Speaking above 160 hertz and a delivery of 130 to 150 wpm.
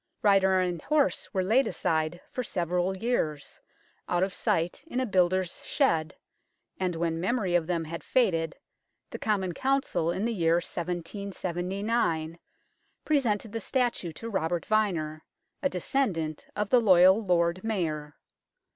Yes: medium, 185 Hz; average, 140 wpm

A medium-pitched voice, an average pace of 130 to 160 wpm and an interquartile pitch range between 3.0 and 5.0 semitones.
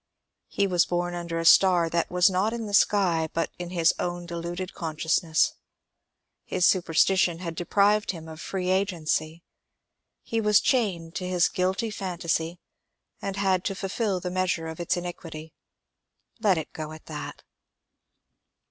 No: medium, 175 Hz; average, 150 wpm; narrow, 2.5 semitones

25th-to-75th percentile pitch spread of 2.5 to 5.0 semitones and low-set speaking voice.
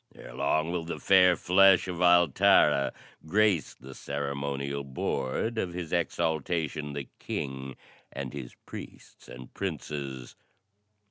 Yes: average, 4.3 semitones; very low, 80 Hz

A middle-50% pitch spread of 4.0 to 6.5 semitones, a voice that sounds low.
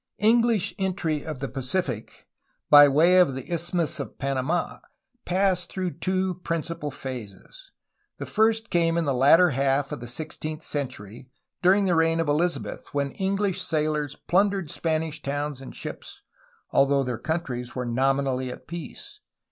No: average, 4.7 semitones; medium, 155 Hz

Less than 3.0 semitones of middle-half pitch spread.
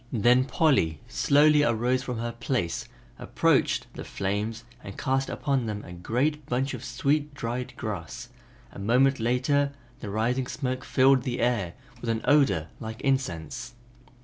No: average, 3.5 semitones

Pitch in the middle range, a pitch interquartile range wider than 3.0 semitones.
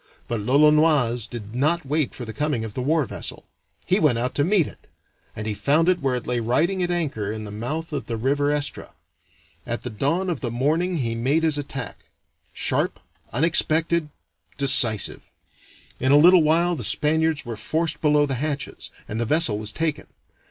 Yes: medium, 145 Hz; average, 5.1 semitones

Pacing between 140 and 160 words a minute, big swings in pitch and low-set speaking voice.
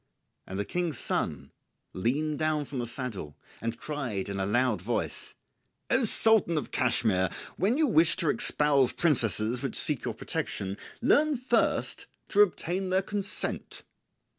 No: average, 145 wpm; wide, 8.4 semitones; medium, 145 Hz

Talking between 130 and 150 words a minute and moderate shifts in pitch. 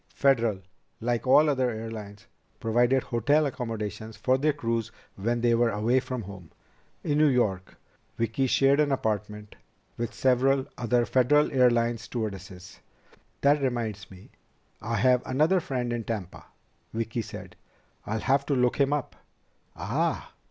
Yes: average, 140 wpm; average, 3.4 semitones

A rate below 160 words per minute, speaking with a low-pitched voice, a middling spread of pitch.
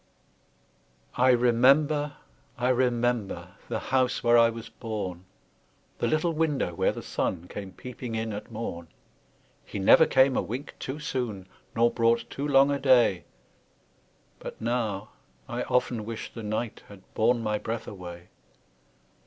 Yes: average, 145 wpm; low, 115 Hz; average, 3.3 semitones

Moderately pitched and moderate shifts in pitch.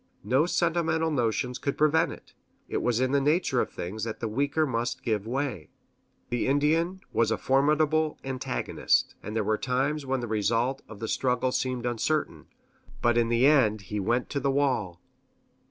No: low, 130 Hz; average, 4.2 semitones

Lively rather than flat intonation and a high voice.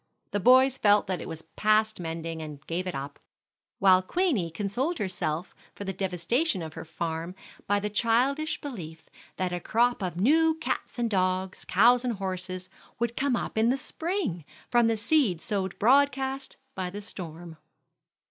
Yes: wide, 5.7 semitones; high, 200 Hz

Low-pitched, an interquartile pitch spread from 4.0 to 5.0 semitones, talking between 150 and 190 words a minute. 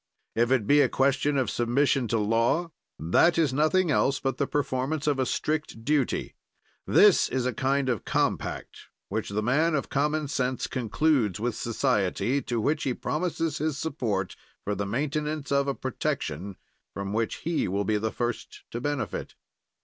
Yes: low, 130 Hz; average, 4.5 semitones; average, 170 wpm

